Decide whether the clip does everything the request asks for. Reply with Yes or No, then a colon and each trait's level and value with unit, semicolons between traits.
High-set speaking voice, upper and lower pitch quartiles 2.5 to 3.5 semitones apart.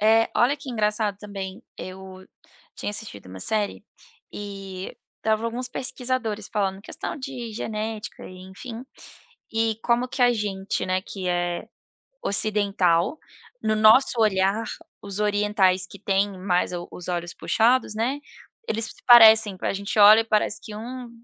Yes: high, 210 Hz; average, 2.9 semitones